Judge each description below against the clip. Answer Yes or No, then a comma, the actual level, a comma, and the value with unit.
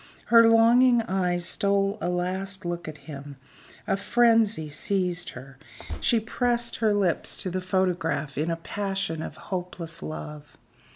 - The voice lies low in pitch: No, medium, 185 Hz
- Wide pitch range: No, average, 4.0 semitones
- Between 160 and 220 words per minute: No, average, 140 wpm